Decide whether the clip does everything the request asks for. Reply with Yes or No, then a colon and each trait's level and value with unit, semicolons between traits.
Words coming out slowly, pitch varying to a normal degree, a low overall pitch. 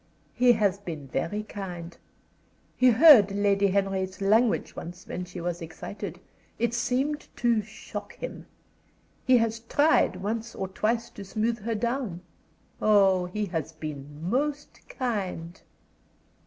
No: slow, 130 wpm; average, 4.5 semitones; high, 205 Hz